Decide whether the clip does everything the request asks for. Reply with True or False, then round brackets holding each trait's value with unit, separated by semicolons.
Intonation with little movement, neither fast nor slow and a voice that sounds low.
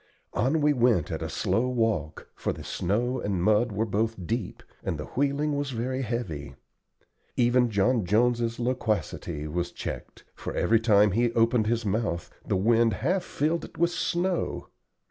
False (3.9 semitones; 165 wpm; 115 Hz)